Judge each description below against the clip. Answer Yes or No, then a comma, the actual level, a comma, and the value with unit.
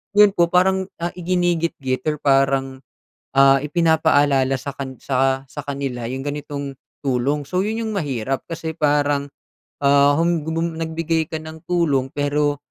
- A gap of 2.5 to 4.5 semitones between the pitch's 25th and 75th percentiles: Yes, average, 3.3 semitones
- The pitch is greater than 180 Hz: No, medium, 145 Hz